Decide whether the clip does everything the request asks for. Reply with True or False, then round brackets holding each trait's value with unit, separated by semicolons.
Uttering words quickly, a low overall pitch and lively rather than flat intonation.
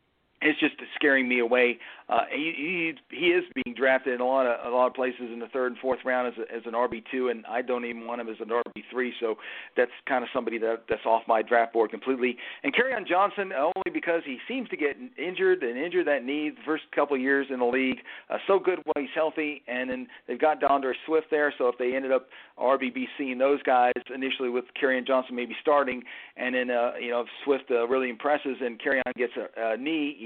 False (240 wpm; 130 Hz; 3.3 semitones)